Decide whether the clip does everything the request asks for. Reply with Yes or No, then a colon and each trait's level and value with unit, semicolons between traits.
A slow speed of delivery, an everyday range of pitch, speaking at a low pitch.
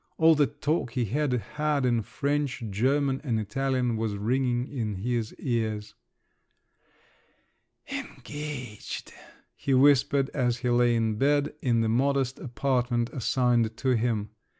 Yes: slow, 125 wpm; average, 3.2 semitones; low, 125 Hz